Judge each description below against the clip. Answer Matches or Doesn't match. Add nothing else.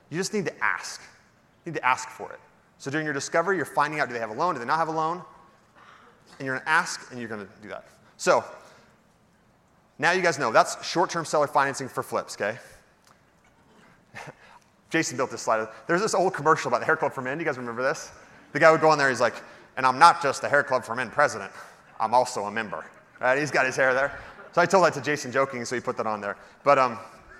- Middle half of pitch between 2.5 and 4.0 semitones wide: Doesn't match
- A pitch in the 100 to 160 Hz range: Matches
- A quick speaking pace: Matches